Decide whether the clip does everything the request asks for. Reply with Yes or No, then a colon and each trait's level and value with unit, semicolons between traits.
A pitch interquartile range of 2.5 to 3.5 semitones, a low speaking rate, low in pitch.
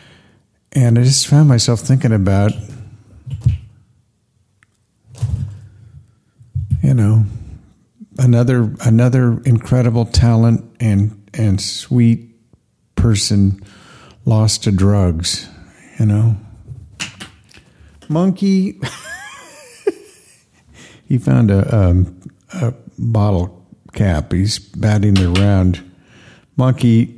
Yes: average, 3.1 semitones; slow, 75 wpm; low, 110 Hz